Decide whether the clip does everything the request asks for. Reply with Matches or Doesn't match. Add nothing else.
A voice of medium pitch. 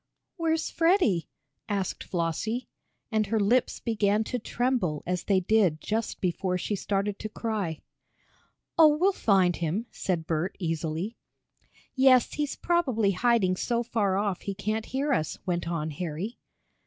Doesn't match